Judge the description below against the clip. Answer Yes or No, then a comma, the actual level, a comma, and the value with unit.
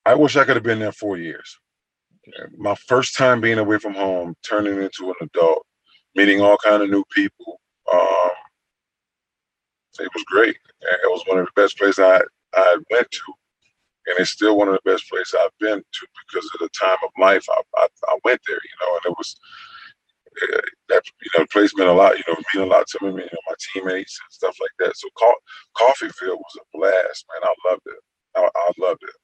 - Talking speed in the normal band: No, fast, 220 wpm